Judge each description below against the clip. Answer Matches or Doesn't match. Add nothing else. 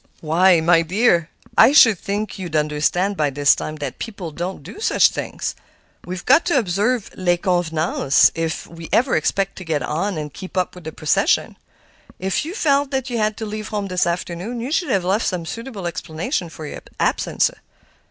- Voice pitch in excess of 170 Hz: Matches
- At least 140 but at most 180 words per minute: Doesn't match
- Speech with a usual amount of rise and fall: Matches